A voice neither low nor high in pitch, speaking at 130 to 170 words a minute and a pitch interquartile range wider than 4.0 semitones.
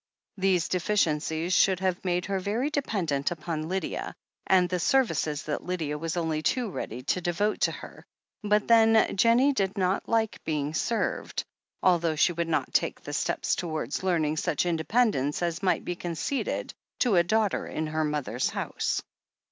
Yes: medium, 175 Hz; average, 165 wpm; average, 4.6 semitones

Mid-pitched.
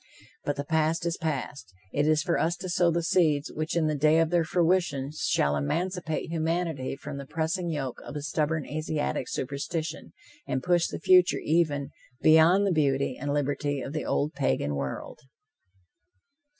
Yes: medium, 155 Hz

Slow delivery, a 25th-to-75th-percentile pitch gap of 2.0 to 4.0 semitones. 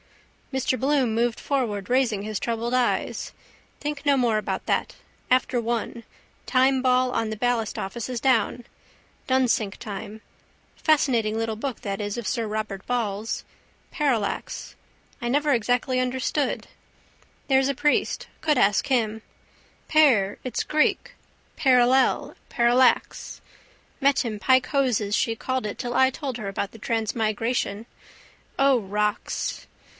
Yes: slow, 130 wpm; average, 3.3 semitones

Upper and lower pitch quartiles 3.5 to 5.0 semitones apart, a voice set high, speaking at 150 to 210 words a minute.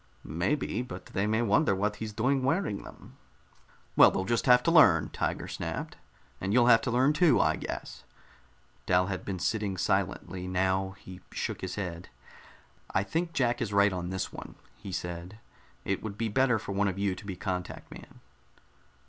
No: average, 4.4 semitones; low, 100 Hz; average, 180 wpm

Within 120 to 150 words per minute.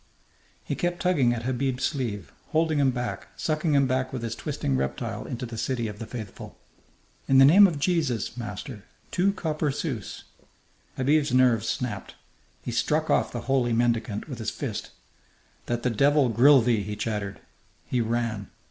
No: average, 165 wpm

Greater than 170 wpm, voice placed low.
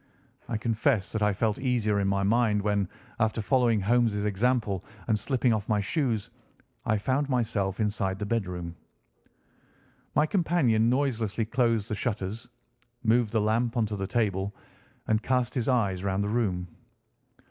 No: average, 150 wpm; low, 110 Hz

